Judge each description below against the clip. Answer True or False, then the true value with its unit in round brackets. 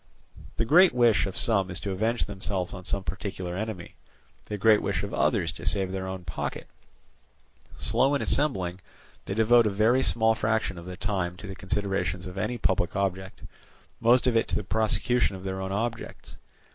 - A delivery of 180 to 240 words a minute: True (185 wpm)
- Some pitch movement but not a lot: True (3.1 semitones)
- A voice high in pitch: False (100 Hz)